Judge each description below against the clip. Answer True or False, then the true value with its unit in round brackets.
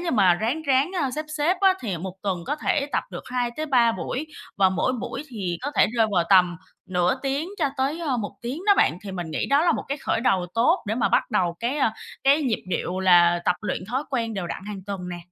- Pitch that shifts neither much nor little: False (7.1 semitones)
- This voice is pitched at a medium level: False (230 Hz)